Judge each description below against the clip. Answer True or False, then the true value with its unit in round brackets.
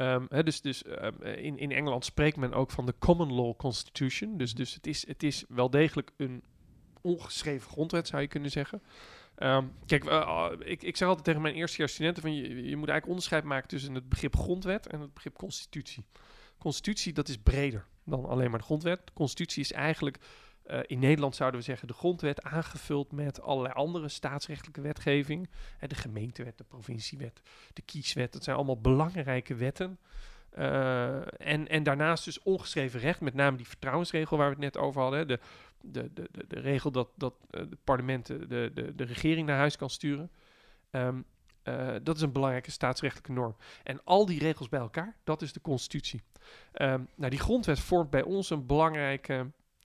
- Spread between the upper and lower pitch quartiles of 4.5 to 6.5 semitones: False (3.2 semitones)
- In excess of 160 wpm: True (195 wpm)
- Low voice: False (145 Hz)